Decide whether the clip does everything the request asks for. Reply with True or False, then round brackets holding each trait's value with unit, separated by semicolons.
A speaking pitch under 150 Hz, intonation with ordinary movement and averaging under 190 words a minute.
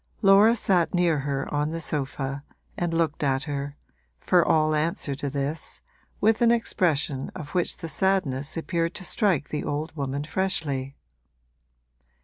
False (155 Hz; 3.9 semitones; 145 wpm)